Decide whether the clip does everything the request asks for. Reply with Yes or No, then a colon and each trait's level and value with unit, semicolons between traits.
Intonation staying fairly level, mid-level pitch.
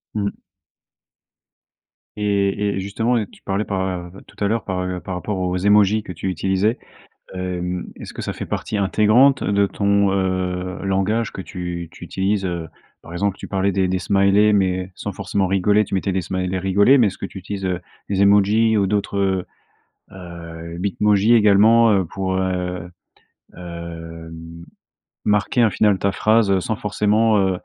No: narrow, 2.1 semitones; very low, 95 Hz